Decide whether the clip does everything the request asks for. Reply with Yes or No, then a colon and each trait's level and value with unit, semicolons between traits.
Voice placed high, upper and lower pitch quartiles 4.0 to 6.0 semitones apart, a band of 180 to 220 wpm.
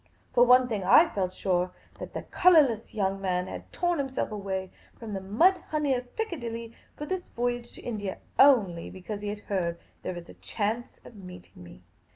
Yes: high, 215 Hz; average, 5.0 semitones; average, 190 wpm